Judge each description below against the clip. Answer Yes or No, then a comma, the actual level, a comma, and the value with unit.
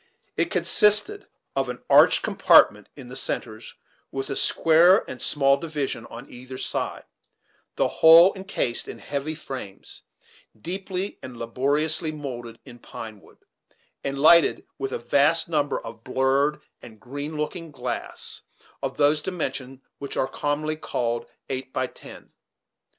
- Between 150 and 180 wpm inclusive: No, average, 140 wpm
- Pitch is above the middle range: No, medium, 140 Hz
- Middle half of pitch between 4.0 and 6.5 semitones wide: No, average, 3.5 semitones